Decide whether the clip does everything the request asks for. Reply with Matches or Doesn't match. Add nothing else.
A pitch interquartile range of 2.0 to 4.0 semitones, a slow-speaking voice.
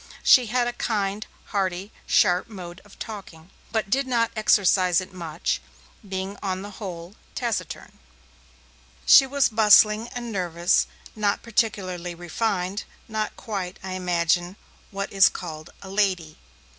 Matches